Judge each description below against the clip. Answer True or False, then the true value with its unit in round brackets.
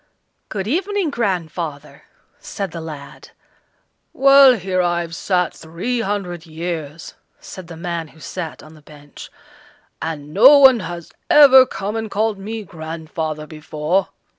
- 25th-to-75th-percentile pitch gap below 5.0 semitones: False (5.4 semitones)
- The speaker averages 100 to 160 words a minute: True (135 wpm)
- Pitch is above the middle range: False (175 Hz)